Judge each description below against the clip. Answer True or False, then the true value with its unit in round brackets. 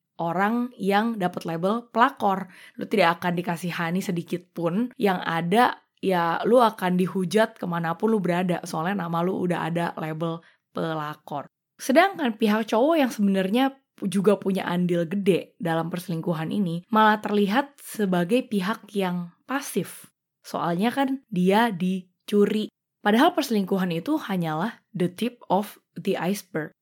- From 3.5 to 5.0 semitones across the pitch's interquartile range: True (4.3 semitones)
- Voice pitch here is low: False (195 Hz)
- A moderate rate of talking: True (130 wpm)